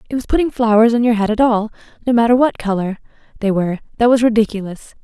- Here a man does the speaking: No, female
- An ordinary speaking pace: No, fast, 215 wpm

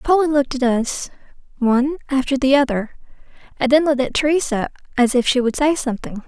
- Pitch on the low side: No, very high, 265 Hz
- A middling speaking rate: Yes, average, 180 wpm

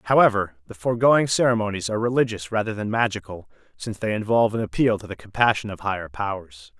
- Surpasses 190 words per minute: No, average, 175 wpm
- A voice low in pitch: Yes, low, 105 Hz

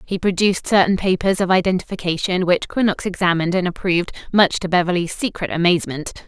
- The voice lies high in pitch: No, medium, 180 Hz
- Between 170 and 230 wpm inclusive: No, average, 155 wpm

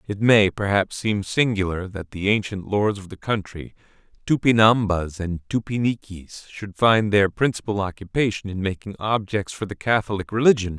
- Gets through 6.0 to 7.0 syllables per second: No, 4.9 syllables/s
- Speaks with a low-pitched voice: Yes, low, 100 Hz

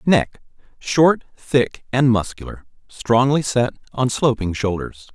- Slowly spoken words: Yes, slow, 105 wpm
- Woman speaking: No, male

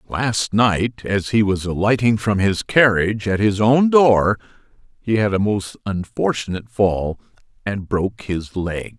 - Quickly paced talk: No, average, 155 wpm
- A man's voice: Yes, male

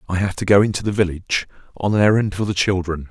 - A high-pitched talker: No, very low, 95 Hz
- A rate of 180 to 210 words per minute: No, fast, 250 wpm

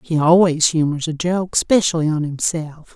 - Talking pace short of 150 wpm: Yes, average, 140 wpm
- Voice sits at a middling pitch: Yes, medium, 165 Hz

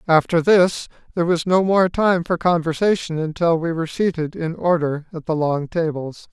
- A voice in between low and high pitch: Yes, medium, 165 Hz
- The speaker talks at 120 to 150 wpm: No, average, 180 wpm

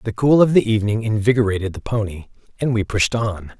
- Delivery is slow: No, average, 200 wpm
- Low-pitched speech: Yes, low, 110 Hz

